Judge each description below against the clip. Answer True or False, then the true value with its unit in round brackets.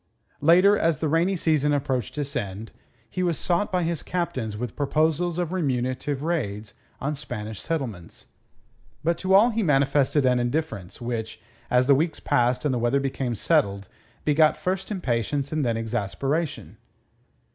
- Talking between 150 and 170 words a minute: True (155 wpm)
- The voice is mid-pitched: True (145 Hz)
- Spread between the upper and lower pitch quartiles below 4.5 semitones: False (5.4 semitones)